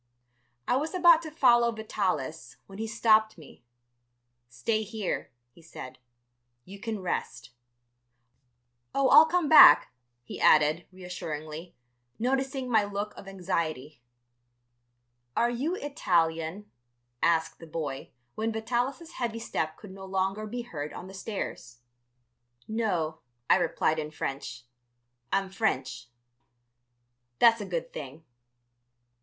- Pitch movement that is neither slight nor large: No, wide, 6.4 semitones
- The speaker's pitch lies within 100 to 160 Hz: No, high, 195 Hz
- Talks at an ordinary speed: No, slow, 120 wpm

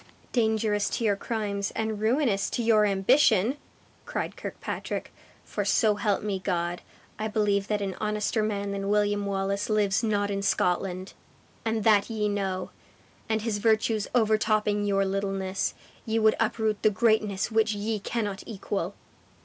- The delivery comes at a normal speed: Yes, average, 150 wpm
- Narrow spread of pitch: Yes, narrow, 1.7 semitones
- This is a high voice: Yes, high, 210 Hz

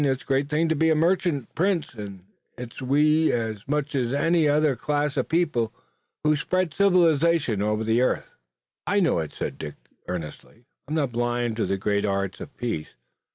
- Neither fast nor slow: Yes, average, 185 wpm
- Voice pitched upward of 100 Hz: Yes, medium, 140 Hz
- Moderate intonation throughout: No, wide, 6.0 semitones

